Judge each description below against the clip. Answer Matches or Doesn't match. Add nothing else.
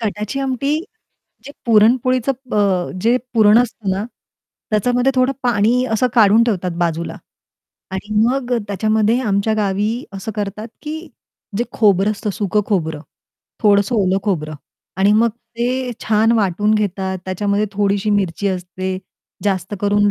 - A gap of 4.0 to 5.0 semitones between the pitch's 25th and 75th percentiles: Doesn't match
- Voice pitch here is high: Matches